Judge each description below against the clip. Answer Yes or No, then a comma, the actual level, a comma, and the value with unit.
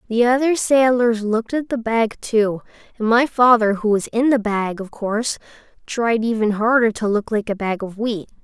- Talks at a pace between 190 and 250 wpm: Yes, average, 200 wpm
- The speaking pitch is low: No, high, 225 Hz